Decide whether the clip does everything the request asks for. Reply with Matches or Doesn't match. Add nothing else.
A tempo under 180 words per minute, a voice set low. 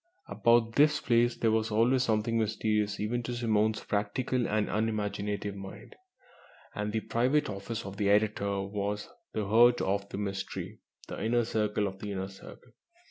Matches